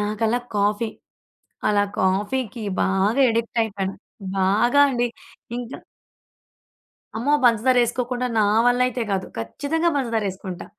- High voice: Yes, high, 225 Hz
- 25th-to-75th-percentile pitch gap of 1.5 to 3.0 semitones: No, average, 3.5 semitones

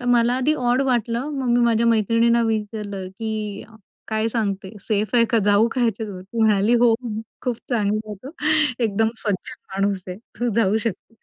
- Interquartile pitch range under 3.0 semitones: Yes, narrow, 2.5 semitones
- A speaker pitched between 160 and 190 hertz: No, high, 220 Hz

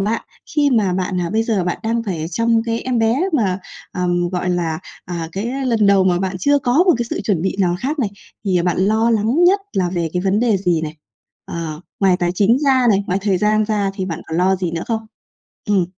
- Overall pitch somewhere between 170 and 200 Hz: Yes, high, 195 Hz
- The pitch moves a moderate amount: Yes, average, 4.3 semitones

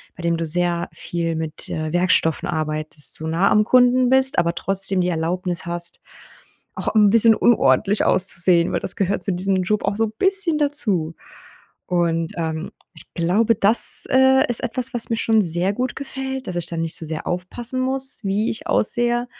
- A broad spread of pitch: Yes, wide, 6.0 semitones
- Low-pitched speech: No, high, 190 Hz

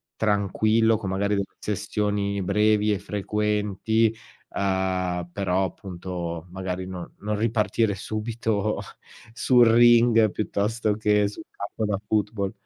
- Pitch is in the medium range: No, low, 105 Hz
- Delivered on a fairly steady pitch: Yes, narrow, 2.2 semitones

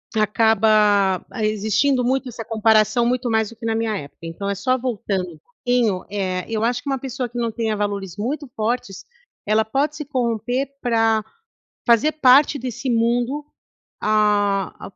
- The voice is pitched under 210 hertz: No, high, 225 Hz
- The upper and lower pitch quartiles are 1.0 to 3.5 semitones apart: Yes, average, 3.0 semitones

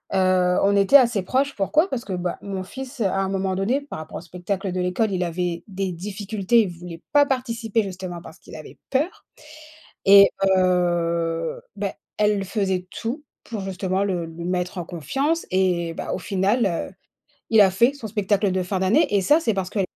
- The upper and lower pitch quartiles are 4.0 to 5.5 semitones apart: No, average, 3.5 semitones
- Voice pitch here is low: No, high, 195 Hz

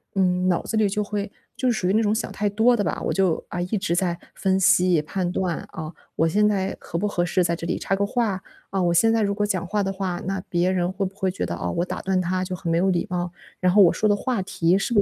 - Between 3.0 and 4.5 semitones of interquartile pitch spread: No, narrow, 2.5 semitones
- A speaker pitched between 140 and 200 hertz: Yes, high, 190 Hz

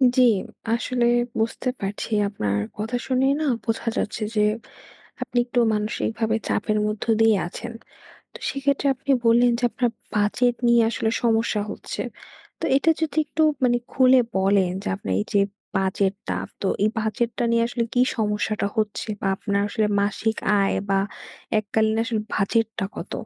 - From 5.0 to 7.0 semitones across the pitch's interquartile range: No, average, 2.7 semitones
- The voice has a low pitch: No, high, 225 Hz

